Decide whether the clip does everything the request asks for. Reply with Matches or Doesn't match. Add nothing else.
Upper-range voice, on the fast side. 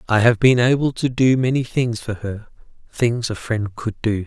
Doesn't match